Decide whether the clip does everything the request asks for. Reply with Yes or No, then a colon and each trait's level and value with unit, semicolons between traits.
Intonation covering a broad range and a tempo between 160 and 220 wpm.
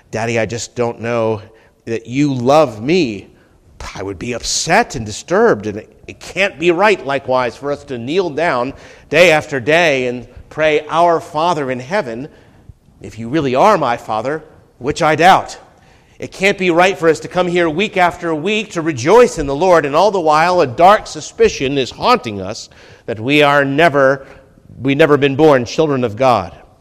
Yes: wide, 6.0 semitones; average, 185 wpm